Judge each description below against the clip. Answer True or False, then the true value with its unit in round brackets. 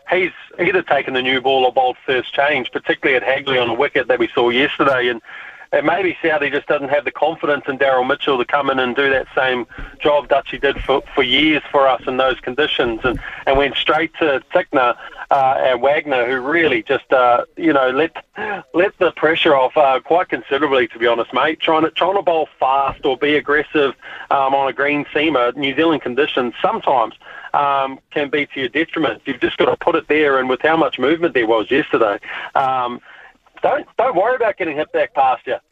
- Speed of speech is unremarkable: False (215 wpm)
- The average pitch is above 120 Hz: True (140 Hz)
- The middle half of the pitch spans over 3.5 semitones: False (2.6 semitones)